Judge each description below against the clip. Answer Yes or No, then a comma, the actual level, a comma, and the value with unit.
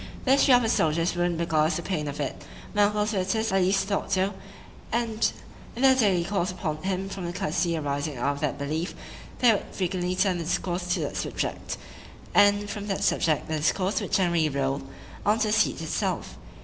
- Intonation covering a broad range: No, average, 4.2 semitones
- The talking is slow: No, average, 195 wpm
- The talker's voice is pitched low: No, medium, 185 Hz